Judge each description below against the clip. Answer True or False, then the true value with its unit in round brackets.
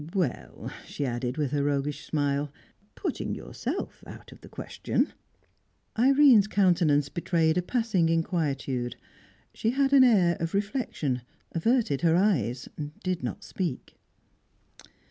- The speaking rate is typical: False (125 wpm)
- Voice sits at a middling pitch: True (165 Hz)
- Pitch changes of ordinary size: False (6.2 semitones)